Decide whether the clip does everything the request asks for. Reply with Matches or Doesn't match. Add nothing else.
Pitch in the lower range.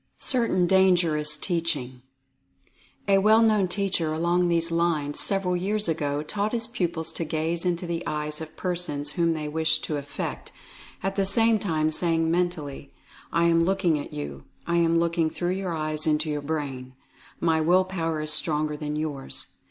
Doesn't match